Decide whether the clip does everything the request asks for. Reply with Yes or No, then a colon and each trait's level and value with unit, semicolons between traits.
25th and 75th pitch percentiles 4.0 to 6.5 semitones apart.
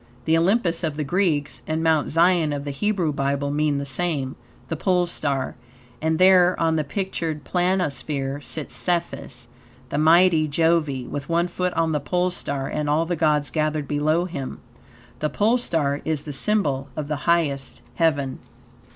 No: average, 3.3 semitones